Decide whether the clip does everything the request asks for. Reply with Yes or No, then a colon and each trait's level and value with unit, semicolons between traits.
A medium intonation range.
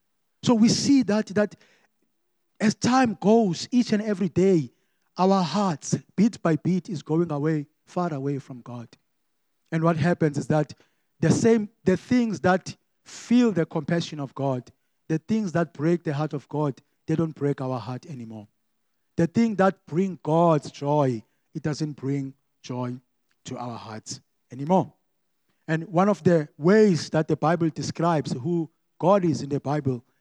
Yes: average, 4.9 semitones